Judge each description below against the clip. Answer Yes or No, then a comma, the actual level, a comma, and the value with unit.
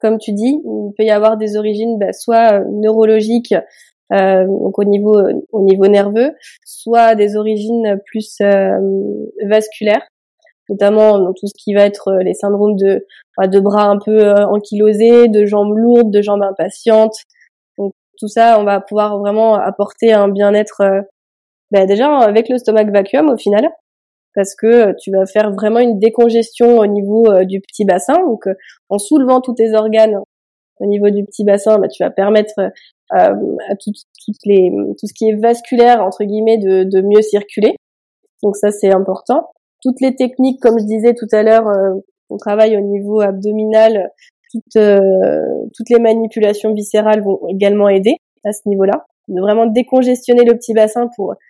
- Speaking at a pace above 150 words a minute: Yes, average, 175 wpm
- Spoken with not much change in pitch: Yes, narrow, 2.1 semitones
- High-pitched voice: Yes, high, 215 Hz